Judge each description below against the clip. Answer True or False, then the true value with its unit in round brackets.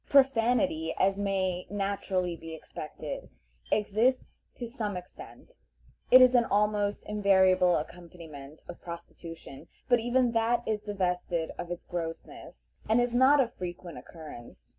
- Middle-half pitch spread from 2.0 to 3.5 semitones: False (5.2 semitones)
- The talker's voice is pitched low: False (195 Hz)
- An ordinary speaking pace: False (130 wpm)